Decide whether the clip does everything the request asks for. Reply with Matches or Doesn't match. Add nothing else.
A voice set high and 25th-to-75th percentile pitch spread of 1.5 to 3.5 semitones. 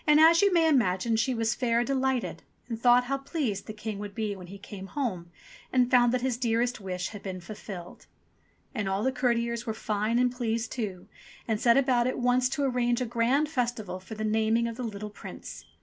Matches